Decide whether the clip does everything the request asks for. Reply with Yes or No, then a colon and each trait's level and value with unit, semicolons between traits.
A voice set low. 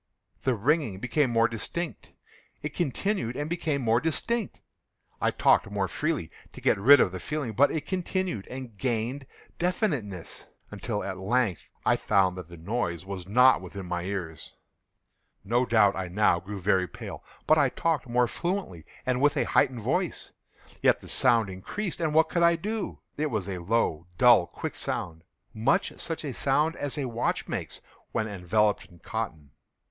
Yes: low, 115 Hz